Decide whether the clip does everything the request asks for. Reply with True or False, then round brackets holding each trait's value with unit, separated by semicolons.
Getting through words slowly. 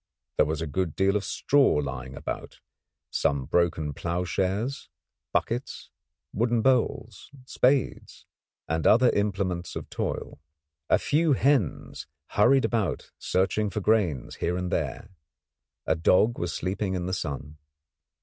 True (130 wpm)